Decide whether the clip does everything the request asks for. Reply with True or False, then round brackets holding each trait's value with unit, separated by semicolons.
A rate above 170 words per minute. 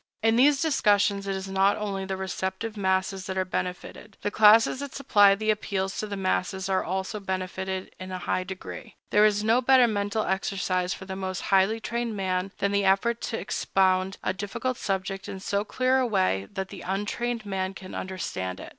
True (195 wpm)